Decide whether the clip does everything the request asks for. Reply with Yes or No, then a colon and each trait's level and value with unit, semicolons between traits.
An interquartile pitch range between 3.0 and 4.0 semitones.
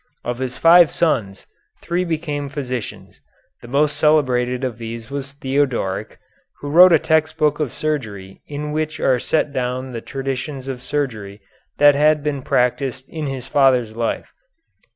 Yes: average, 3.4 semitones